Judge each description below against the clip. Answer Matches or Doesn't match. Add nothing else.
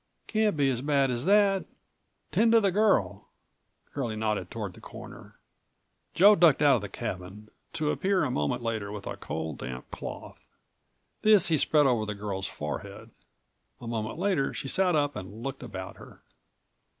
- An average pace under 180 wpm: Matches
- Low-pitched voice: Matches